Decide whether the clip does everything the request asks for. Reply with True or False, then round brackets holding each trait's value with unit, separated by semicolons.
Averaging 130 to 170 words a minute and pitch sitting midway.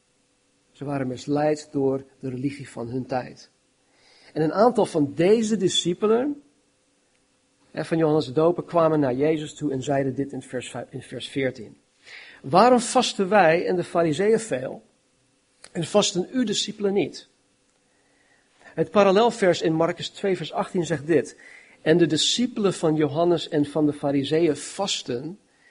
True (140 wpm; 160 Hz)